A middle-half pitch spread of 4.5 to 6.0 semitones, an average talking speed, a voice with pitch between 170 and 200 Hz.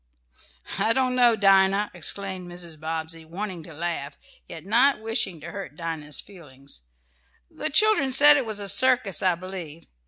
Yes: average, 5.3 semitones; average, 160 wpm; high, 190 Hz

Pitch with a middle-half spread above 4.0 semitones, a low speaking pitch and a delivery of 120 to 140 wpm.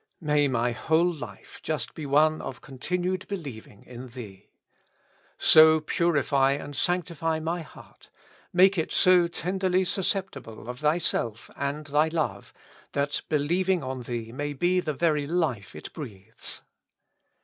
No: average, 4.9 semitones; medium, 150 Hz; slow, 135 wpm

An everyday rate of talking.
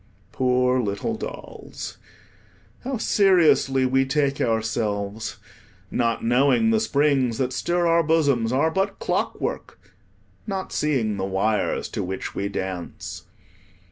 No: slow, 115 wpm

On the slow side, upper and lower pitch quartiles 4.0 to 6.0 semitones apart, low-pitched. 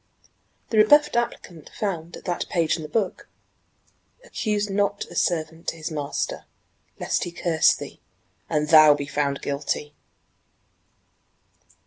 No: slow, 130 wpm; average, 5.0 semitones; medium, 165 Hz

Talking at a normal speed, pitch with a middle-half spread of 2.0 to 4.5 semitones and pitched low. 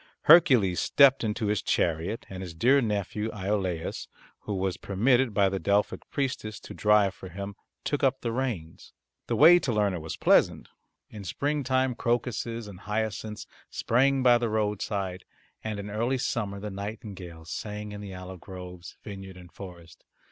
Yes: average, 160 wpm; average, 3.9 semitones; low, 105 Hz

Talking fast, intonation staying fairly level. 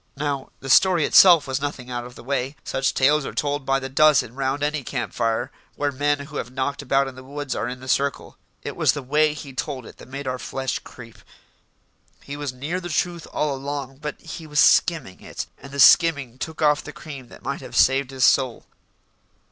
Yes: fast, 220 wpm; narrow, 2.1 semitones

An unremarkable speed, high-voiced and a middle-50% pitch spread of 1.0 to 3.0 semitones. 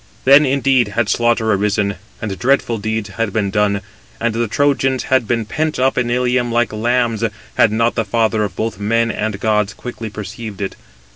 No: average, 185 wpm; low, 115 Hz; narrow, 2.6 semitones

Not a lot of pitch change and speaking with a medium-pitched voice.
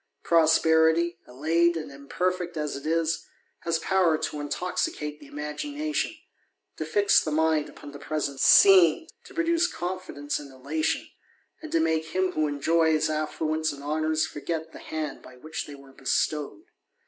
Yes: narrow, 2.3 semitones; medium, 160 Hz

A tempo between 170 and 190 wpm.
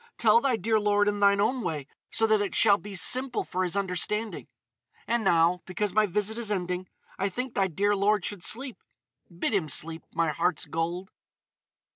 Yes: average, 175 wpm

